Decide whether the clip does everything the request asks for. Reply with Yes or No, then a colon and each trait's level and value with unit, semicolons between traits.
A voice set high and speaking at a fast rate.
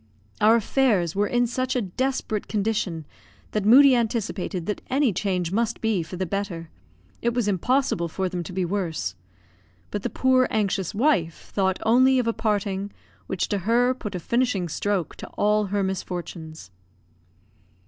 No: high, 205 Hz; average, 160 wpm